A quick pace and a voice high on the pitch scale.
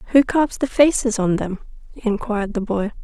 No: average, 180 wpm; high, 225 Hz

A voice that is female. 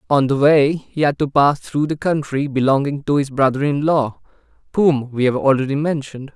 No: male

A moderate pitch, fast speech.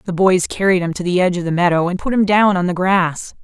Yes: medium, 180 Hz; fast, 295 wpm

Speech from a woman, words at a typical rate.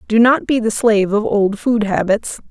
No: female; fast, 215 wpm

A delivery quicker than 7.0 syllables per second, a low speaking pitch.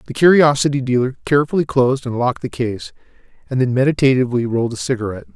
Yes: 7.4 syllables/s; low, 130 Hz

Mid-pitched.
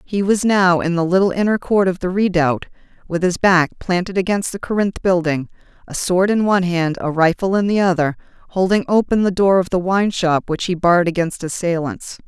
Yes: medium, 180 Hz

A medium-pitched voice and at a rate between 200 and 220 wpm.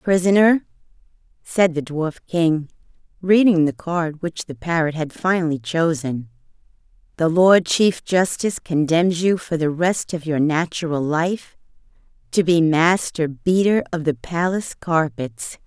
No: medium, 165 Hz; slow, 135 wpm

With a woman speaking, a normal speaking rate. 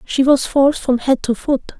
No: female; fast, 235 wpm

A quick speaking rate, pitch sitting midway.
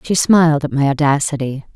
No: average, 170 wpm; medium, 150 Hz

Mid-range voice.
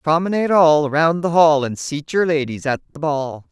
Yes: medium, 155 Hz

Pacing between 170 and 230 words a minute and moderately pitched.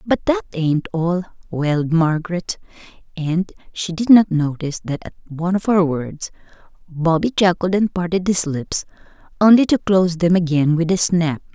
No: average, 160 wpm; medium, 175 Hz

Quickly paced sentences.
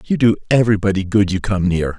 Yes: fast, 210 wpm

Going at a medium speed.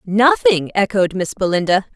No: slow, 125 wpm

